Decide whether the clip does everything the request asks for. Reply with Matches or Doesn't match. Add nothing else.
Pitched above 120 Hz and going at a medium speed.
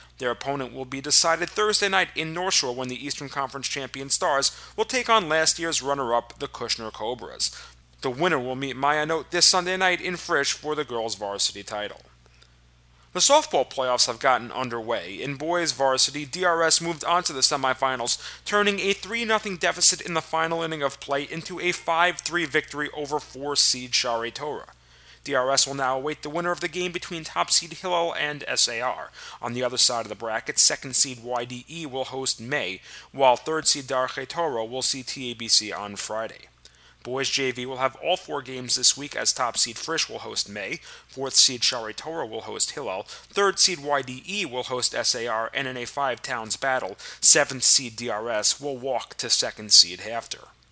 Matches